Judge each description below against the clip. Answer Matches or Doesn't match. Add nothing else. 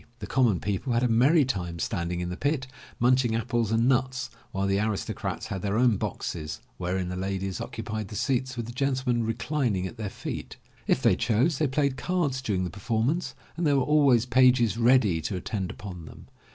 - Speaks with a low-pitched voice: Matches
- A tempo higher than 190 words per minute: Matches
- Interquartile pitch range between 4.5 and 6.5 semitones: Matches